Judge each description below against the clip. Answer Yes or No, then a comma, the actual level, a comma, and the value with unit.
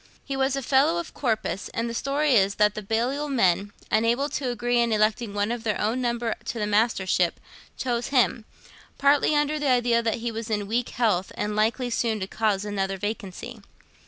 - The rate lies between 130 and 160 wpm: No, average, 195 wpm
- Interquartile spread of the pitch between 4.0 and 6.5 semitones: No, average, 3.2 semitones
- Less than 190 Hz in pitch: No, high, 230 Hz